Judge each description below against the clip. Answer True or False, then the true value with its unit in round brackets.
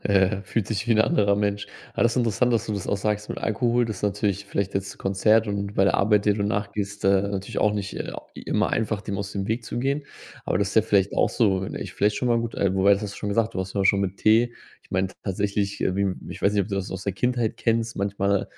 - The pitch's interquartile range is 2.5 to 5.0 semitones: False (1.9 semitones)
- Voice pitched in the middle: False (100 Hz)